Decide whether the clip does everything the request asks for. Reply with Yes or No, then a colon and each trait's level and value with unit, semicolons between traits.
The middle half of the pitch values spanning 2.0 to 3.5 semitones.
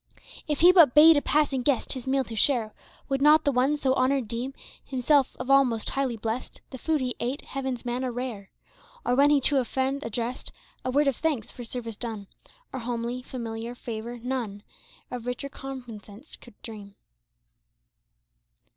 Yes: average, 2.8 semitones